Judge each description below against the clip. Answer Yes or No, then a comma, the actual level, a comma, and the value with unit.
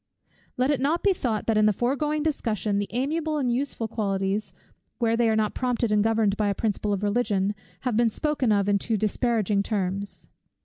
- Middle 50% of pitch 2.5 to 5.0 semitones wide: Yes, average, 3.6 semitones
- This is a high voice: Yes, high, 225 Hz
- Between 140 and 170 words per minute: No, average, 195 wpm